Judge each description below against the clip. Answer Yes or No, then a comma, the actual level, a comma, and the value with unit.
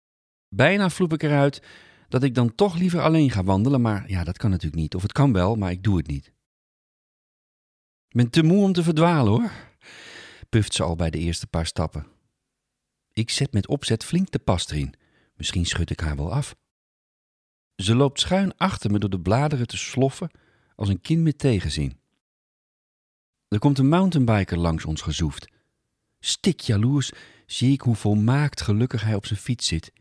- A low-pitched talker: Yes, low, 110 Hz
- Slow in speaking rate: No, average, 180 wpm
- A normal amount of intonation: No, wide, 7.2 semitones